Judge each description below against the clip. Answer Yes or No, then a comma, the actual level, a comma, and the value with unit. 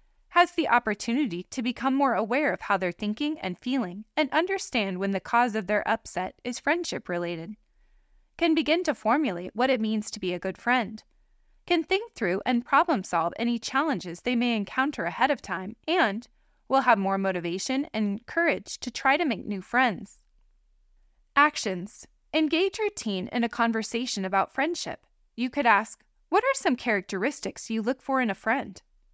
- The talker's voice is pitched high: Yes, high, 240 Hz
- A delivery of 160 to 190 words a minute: Yes, average, 175 wpm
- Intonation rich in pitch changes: Yes, wide, 5.8 semitones